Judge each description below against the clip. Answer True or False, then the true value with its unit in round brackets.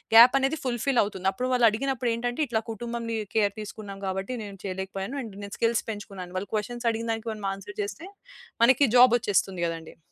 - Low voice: False (225 Hz)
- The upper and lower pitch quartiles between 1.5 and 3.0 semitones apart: False (3.7 semitones)